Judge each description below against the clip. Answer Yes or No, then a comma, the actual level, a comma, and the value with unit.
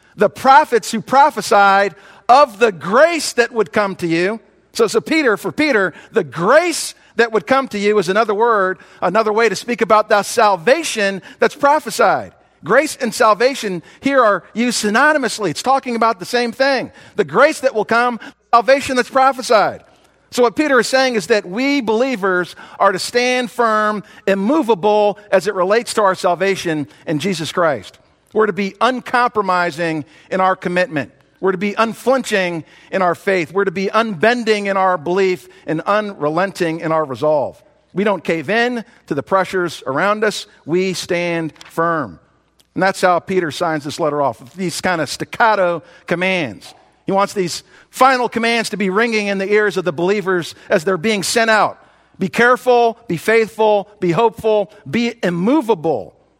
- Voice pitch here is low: No, high, 210 Hz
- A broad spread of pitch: No, average, 4.4 semitones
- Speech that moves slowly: No, average, 170 wpm